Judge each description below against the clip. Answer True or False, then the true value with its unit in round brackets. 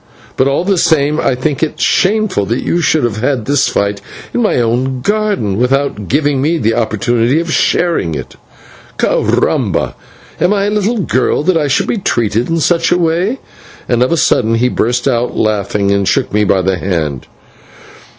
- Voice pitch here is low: True (130 Hz)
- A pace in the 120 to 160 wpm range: False (185 wpm)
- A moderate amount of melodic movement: False (7.3 semitones)